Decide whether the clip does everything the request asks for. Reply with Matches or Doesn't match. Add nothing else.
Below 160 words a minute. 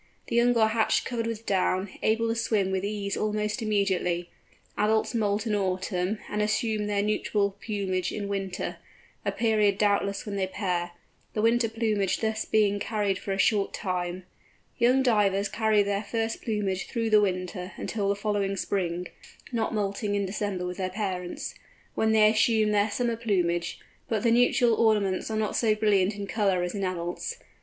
Doesn't match